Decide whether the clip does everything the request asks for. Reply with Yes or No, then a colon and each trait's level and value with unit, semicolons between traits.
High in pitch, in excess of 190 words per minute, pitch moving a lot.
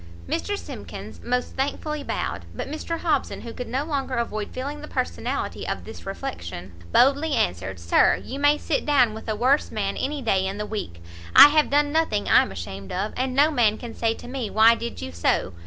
Yes: high, 245 Hz; fast, 205 wpm; wide, 5.7 semitones